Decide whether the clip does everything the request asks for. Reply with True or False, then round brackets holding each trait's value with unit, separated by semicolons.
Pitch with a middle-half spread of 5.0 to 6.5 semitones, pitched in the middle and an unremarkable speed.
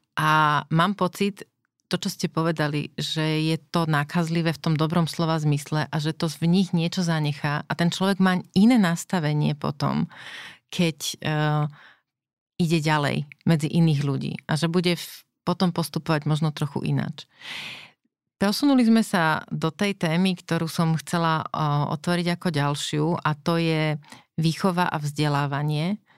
False (2.6 semitones; 165 Hz; 150 wpm)